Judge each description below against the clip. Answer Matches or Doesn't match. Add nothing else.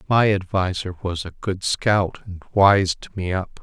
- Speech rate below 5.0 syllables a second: Matches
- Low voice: Matches